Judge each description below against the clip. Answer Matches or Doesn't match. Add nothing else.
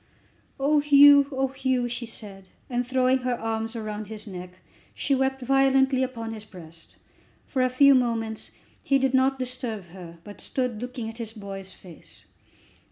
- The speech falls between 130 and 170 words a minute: Matches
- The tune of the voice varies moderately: Matches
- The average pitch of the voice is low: Doesn't match